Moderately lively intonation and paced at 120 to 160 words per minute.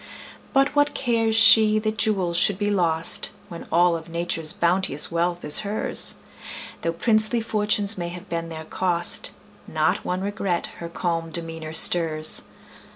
Yes: average, 4.2 semitones; average, 150 wpm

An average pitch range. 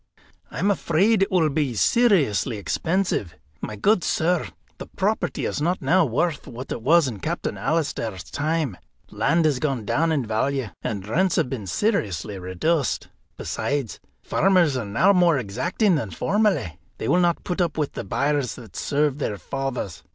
No: wide, 7.3 semitones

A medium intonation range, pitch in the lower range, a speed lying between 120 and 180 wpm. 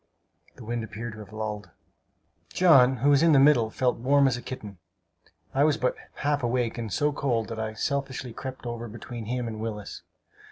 No: average, 3.6 semitones; low, 120 Hz; average, 195 wpm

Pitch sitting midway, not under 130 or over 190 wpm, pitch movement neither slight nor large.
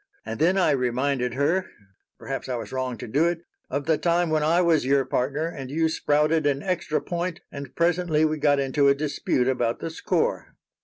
No: medium, 150 Hz; average, 200 wpm; average, 3.5 semitones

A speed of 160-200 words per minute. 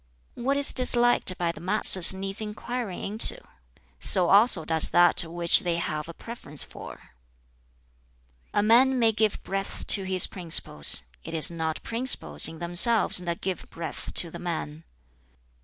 No: average, 150 wpm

